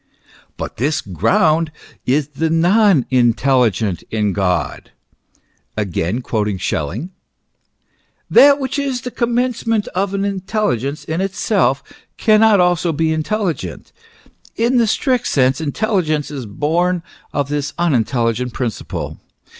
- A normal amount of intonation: No, wide, 8.5 semitones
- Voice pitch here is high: No, medium, 160 Hz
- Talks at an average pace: No, slow, 115 wpm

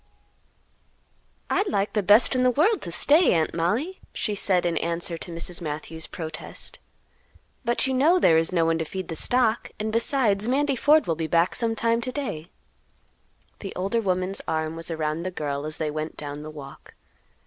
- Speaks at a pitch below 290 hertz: Yes, medium, 185 Hz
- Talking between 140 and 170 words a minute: No, average, 185 wpm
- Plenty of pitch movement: Yes, wide, 6.6 semitones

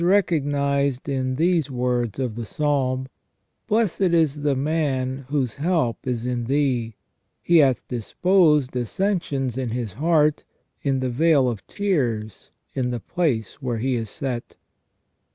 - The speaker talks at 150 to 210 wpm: No, average, 140 wpm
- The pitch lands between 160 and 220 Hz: No, low, 135 Hz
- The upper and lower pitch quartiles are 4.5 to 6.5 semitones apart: No, average, 3.7 semitones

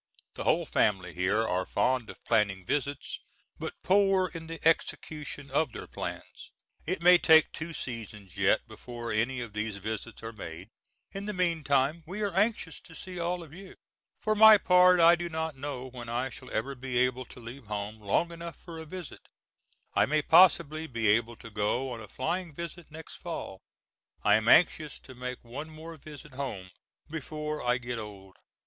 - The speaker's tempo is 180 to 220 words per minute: Yes, average, 185 wpm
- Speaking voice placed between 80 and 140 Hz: Yes, low, 135 Hz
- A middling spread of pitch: No, wide, 6.6 semitones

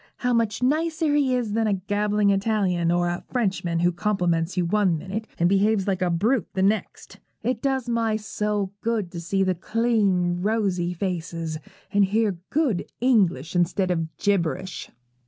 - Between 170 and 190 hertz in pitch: No, high, 200 Hz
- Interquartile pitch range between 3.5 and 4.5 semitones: Yes, average, 4.0 semitones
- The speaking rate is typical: Yes, average, 165 wpm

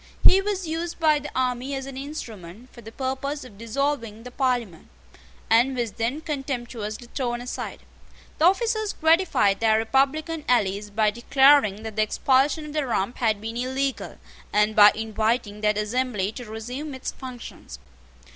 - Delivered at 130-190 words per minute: Yes, average, 155 wpm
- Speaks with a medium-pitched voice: No, very high, 250 Hz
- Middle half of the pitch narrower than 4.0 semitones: No, average, 4.3 semitones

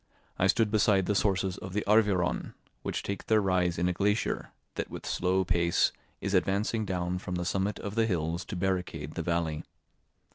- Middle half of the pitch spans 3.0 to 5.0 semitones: No, narrow, 2.6 semitones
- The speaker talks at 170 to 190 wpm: Yes, average, 185 wpm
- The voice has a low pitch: Yes, very low, 95 Hz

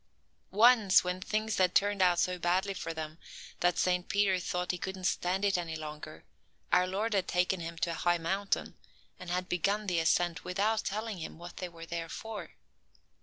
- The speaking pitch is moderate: Yes, medium, 180 Hz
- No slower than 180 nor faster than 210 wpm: Yes, average, 190 wpm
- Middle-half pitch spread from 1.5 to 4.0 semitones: Yes, narrow, 2.6 semitones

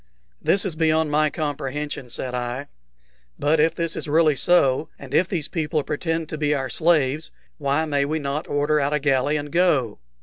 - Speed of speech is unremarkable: Yes, average, 190 wpm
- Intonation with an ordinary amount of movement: No, narrow, 2.2 semitones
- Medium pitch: Yes, medium, 150 Hz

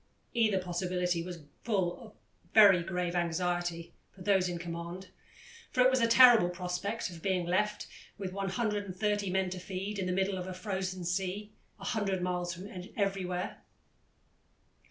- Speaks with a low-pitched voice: No, medium, 185 Hz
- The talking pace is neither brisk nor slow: Yes, average, 155 wpm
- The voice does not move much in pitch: Yes, narrow, 2.3 semitones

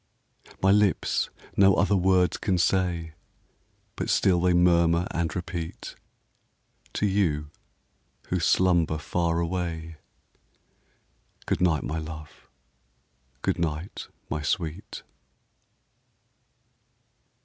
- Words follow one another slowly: Yes, slow, 95 wpm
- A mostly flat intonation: Yes, narrow, 2.2 semitones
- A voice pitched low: Yes, very low, 85 Hz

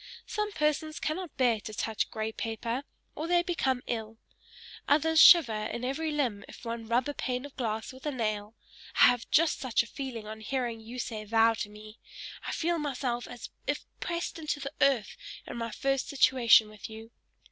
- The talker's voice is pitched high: Yes, high, 245 Hz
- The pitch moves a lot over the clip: No, average, 4.6 semitones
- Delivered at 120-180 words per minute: No, average, 190 wpm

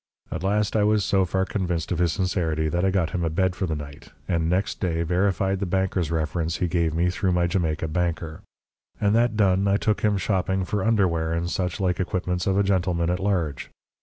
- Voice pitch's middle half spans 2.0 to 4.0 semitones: Yes, narrow, 2.6 semitones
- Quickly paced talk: Yes, fast, 220 wpm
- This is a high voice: No, very low, 90 Hz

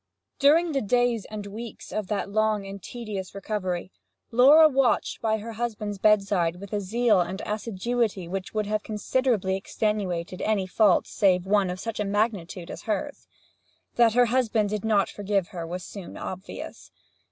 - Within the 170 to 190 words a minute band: No, average, 160 wpm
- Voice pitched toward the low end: No, high, 210 Hz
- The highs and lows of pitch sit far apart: No, average, 3.0 semitones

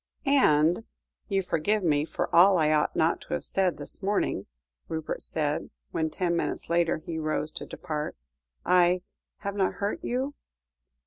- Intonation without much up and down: No, average, 3.9 semitones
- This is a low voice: No, medium, 170 Hz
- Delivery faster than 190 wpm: No, average, 155 wpm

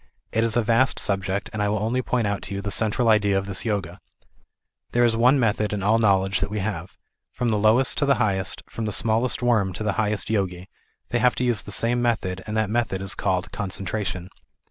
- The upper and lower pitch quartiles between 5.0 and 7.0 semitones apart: No, average, 3.0 semitones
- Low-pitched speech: Yes, low, 105 Hz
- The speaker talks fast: Yes, fast, 230 wpm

